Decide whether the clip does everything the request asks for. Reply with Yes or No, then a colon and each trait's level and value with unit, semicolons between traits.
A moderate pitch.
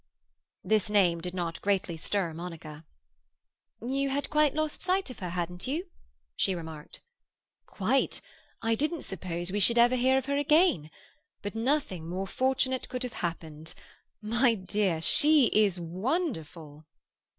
No: high, 205 Hz